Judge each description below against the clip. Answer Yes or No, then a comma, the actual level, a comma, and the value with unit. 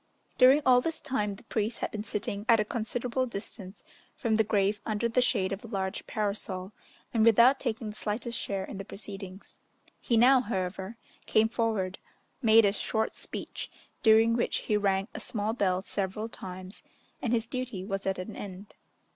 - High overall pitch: Yes, high, 215 Hz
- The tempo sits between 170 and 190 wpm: Yes, average, 180 wpm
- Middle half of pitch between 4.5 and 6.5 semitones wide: No, average, 2.9 semitones